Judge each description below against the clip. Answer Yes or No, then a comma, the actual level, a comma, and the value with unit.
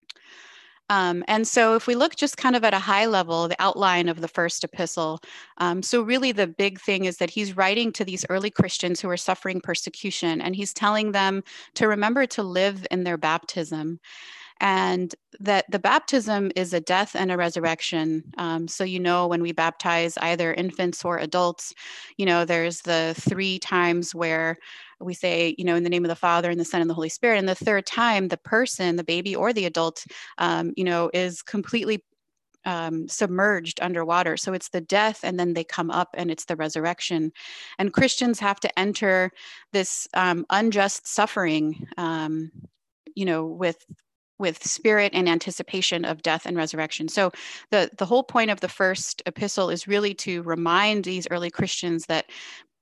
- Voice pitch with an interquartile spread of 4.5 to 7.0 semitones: No, average, 2.8 semitones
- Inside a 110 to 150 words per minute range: No, average, 185 wpm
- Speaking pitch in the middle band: Yes, medium, 180 Hz